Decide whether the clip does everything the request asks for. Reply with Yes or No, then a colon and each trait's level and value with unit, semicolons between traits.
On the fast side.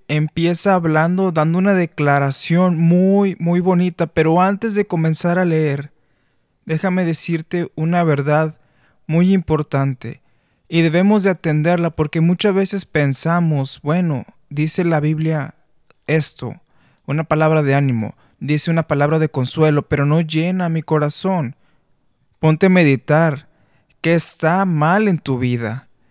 No: average, 130 wpm